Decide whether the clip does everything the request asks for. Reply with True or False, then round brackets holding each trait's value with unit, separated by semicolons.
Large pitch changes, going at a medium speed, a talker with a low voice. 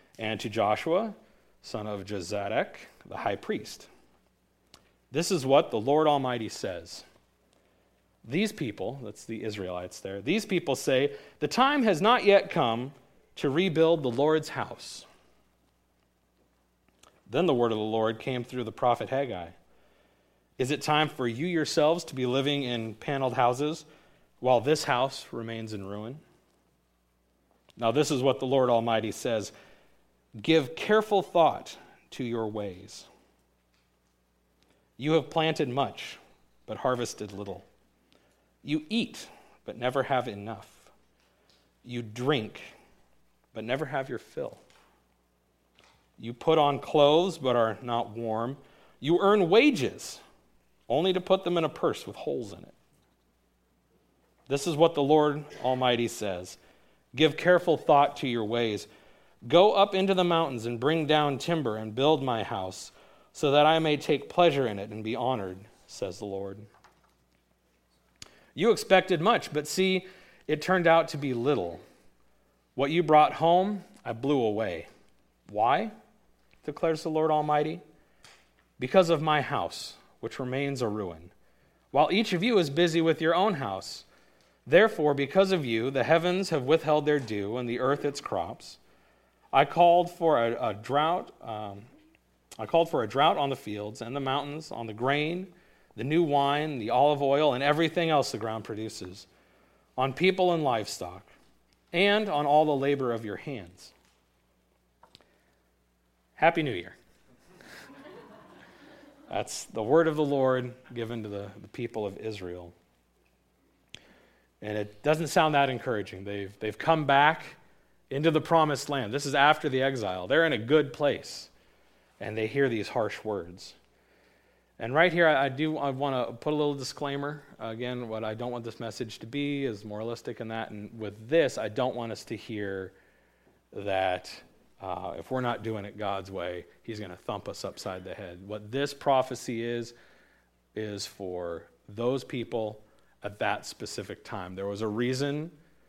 True (7.0 semitones; 155 wpm; 125 Hz)